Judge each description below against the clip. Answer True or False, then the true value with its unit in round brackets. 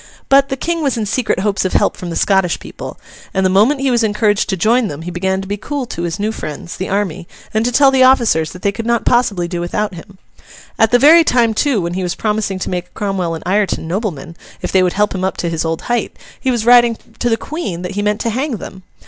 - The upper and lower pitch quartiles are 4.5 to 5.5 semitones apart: True (4.8 semitones)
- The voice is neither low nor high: False (205 Hz)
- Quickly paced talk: True (260 wpm)